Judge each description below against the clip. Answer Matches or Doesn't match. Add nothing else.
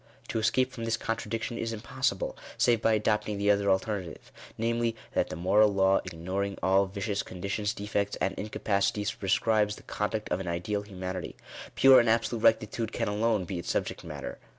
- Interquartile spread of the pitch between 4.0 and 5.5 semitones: Doesn't match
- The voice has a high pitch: Doesn't match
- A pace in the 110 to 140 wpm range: Doesn't match